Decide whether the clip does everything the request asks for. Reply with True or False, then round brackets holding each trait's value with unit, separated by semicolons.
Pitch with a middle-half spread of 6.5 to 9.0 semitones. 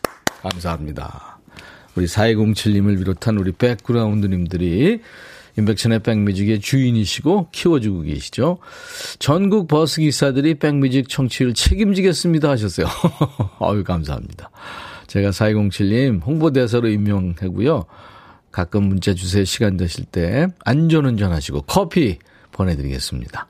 True (7.2 semitones)